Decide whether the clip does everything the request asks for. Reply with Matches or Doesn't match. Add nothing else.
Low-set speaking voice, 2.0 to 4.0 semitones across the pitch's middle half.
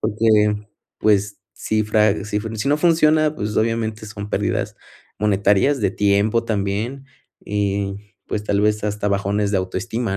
Doesn't match